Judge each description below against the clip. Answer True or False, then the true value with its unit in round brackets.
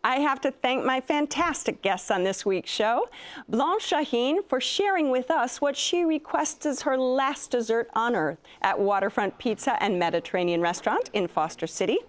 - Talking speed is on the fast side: False (175 wpm)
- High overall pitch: True (255 Hz)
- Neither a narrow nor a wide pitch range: False (6.6 semitones)